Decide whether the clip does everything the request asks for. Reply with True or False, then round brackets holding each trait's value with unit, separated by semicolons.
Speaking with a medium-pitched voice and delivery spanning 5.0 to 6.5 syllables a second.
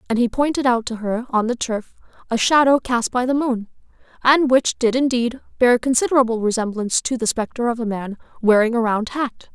False (240 Hz; 5.5 syllables/s)